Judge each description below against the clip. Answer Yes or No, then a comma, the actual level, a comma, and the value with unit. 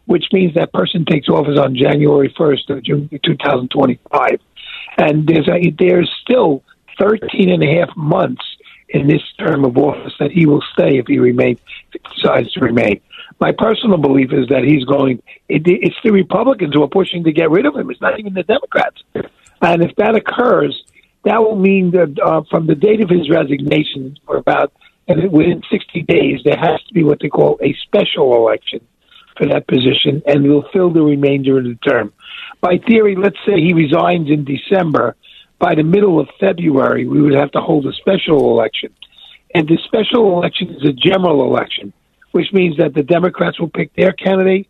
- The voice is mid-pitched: Yes, medium, 165 Hz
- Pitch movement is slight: No, average, 4.1 semitones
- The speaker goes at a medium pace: Yes, average, 190 wpm